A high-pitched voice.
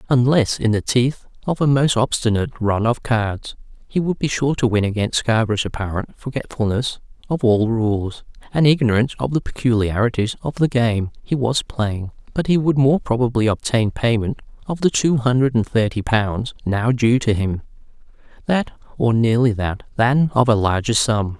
No: low, 120 Hz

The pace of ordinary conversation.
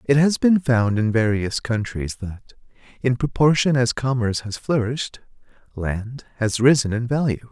Yes: average, 150 wpm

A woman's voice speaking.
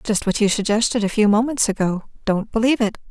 Yes: female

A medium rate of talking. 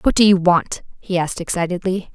Yes: average, 195 wpm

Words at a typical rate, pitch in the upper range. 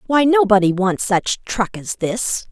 Yes: average, 165 wpm; high, 215 Hz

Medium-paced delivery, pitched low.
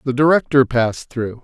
Yes: average, 165 wpm; low, 130 Hz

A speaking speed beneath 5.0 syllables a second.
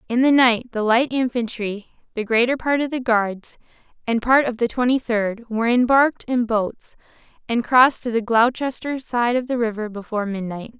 No: 5.1 syllables/s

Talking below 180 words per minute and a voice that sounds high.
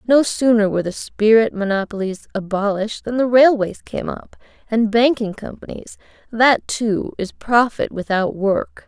Yes: average, 140 wpm; high, 220 Hz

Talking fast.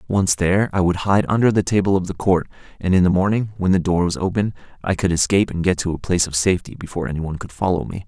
Yes: fast, 260 wpm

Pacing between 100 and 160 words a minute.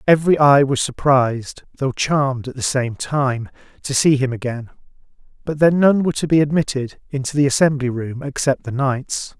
No: average, 180 wpm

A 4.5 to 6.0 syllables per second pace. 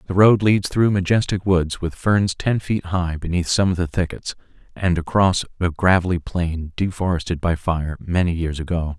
Yes: 4.8 syllables/s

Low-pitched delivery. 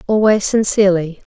No: high, 200 Hz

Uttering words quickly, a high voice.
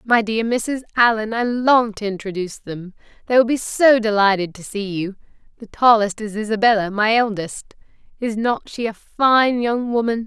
No: average, 175 wpm; high, 220 Hz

